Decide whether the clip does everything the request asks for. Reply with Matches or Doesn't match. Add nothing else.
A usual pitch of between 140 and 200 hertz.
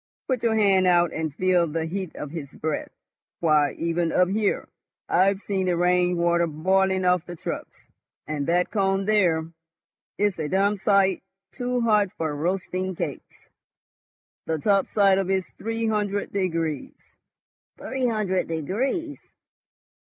Matches